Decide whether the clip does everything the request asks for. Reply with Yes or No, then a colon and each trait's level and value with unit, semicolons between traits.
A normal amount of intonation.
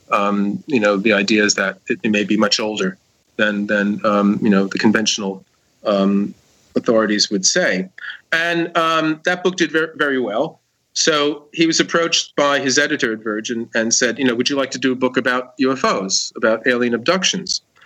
No: wide, 6.0 semitones